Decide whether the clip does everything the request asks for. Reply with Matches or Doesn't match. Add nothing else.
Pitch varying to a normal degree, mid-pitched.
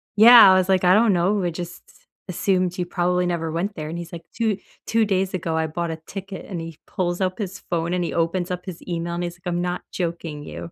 Doesn't match